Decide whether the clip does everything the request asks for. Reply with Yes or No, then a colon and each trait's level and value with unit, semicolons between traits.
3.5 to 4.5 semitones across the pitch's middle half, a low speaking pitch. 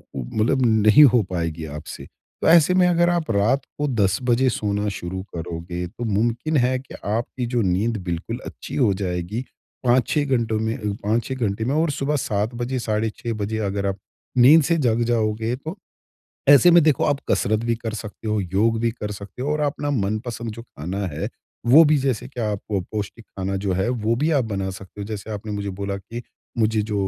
Yes: average, 4.2 semitones; low, 110 Hz